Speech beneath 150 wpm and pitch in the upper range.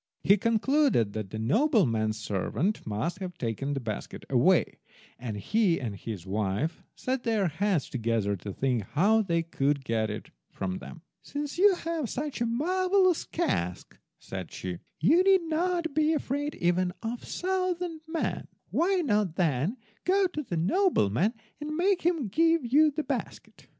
No: average, 160 wpm; high, 210 Hz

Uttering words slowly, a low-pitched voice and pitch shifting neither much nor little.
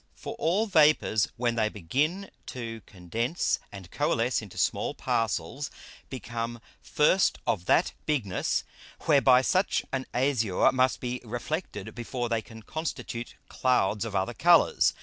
Yes: slow, 130 wpm; low, 120 Hz; average, 4.6 semitones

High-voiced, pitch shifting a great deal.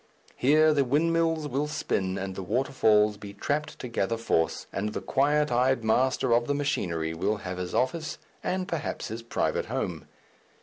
No: low, 125 Hz; wide, 6.0 semitones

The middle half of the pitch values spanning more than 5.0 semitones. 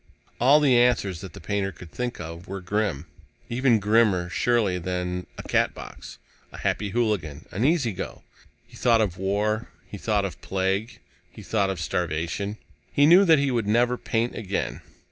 No: average, 4.6 semitones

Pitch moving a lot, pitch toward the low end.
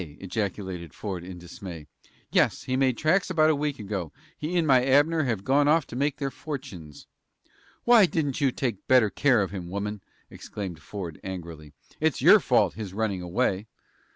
Yes: wide, 7.5 semitones; low, 110 Hz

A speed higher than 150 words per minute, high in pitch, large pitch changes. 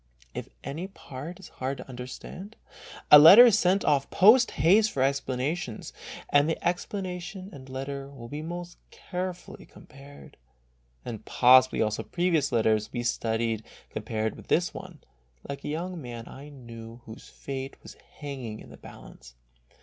No: average, 160 wpm; medium, 140 Hz; wide, 6.3 semitones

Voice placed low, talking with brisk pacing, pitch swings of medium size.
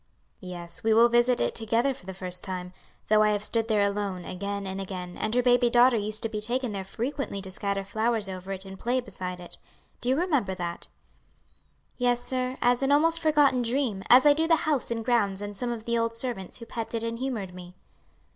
No: high, 225 Hz; fast, 220 wpm; average, 4.2 semitones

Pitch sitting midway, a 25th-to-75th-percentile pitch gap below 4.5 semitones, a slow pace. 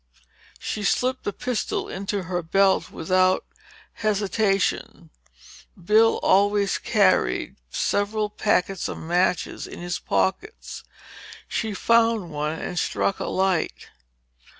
No: high, 195 Hz; average, 2.9 semitones; slow, 105 wpm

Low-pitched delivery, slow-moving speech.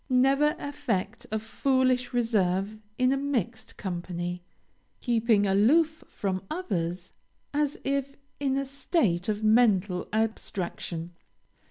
No: high, 225 Hz; slow, 110 wpm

